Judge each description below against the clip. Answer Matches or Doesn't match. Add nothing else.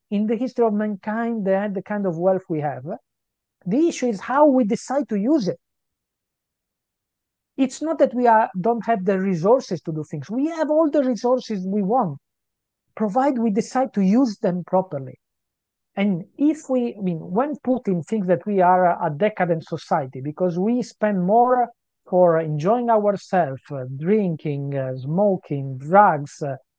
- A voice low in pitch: Doesn't match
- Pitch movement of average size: Doesn't match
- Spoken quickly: Doesn't match